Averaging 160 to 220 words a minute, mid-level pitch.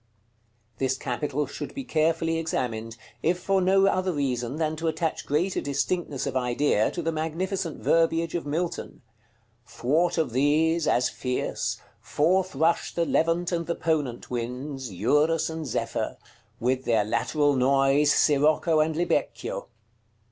No: average, 140 wpm; medium, 155 Hz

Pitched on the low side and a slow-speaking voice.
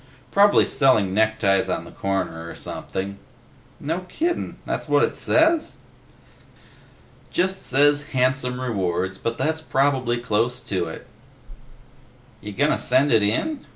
Yes: low, 125 Hz; slow, 125 wpm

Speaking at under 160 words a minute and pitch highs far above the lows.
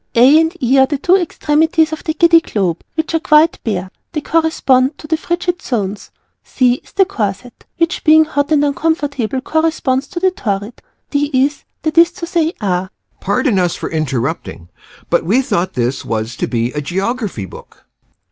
No: average, 180 wpm; wide, 8.4 semitones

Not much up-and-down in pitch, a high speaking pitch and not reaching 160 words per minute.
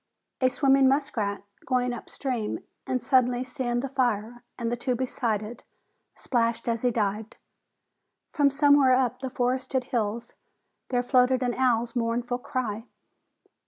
Yes: narrow, 2.0 semitones; high, 245 Hz; average, 140 wpm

